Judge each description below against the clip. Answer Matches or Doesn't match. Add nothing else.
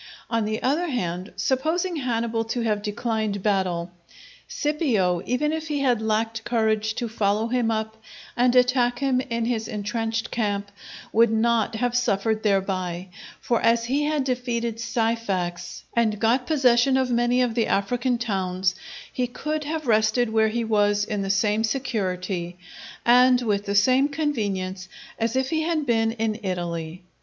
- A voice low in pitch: Doesn't match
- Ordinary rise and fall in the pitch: Matches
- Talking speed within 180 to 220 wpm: Doesn't match